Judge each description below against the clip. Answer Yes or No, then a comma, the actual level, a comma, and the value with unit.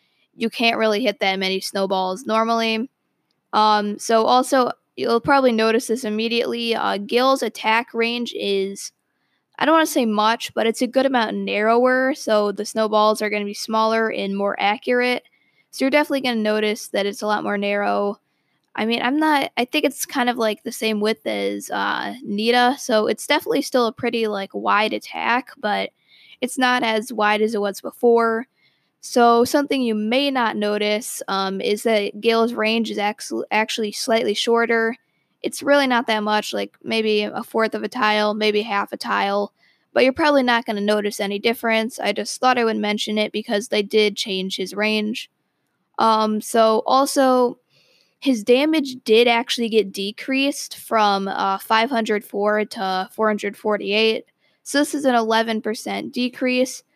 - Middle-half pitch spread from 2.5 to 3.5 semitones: Yes, average, 2.8 semitones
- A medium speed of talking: Yes, average, 170 wpm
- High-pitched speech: Yes, high, 225 Hz